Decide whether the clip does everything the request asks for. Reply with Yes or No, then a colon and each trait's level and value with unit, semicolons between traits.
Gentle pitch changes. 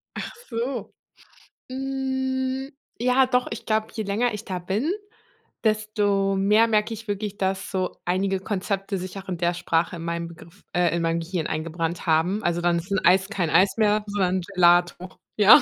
No: average, 3.7 semitones